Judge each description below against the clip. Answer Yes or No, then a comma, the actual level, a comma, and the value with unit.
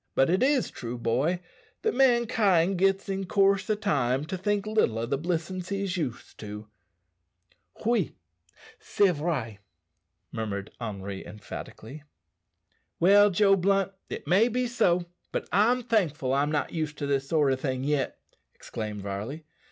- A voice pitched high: No, medium, 170 Hz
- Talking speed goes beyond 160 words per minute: No, average, 145 wpm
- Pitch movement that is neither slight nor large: No, wide, 7.2 semitones